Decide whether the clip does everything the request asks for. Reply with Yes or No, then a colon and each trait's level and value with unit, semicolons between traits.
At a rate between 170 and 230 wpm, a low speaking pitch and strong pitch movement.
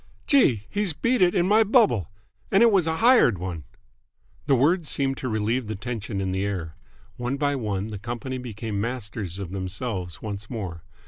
Yes: average, 185 wpm; low, 115 Hz; wide, 7.0 semitones